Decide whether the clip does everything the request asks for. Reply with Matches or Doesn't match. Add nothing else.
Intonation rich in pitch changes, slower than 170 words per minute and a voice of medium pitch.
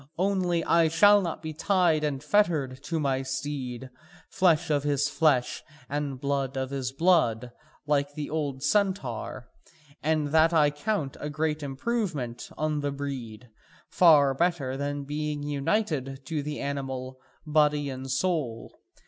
Doesn't match